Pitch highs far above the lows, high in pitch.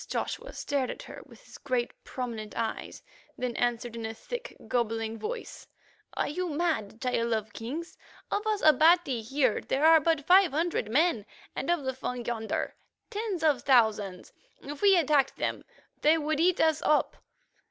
Yes: wide, 6.1 semitones; very high, 275 Hz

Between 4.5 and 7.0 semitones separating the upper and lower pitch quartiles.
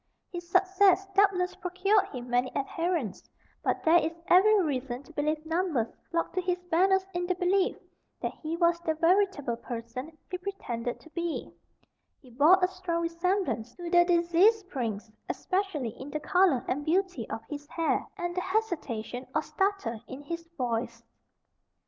Yes: average, 5.3 semitones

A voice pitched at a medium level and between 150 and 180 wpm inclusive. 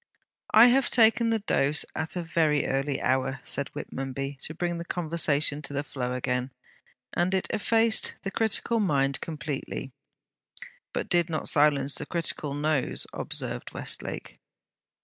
No: medium, 150 Hz; average, 140 wpm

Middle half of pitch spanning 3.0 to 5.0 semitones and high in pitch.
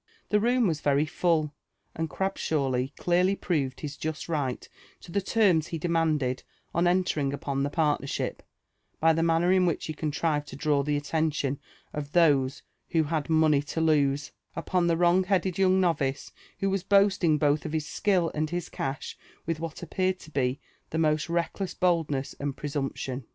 No: average, 3.4 semitones; medium, 160 Hz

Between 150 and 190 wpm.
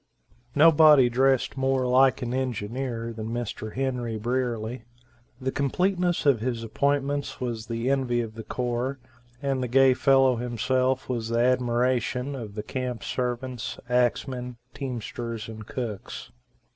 No: slow, 135 wpm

